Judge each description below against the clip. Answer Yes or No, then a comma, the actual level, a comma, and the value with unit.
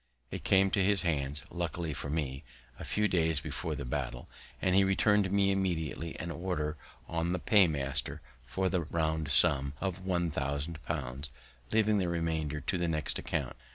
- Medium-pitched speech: No, very low, 85 Hz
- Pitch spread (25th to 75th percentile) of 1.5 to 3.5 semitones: No, average, 4.1 semitones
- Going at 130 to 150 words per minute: No, average, 170 wpm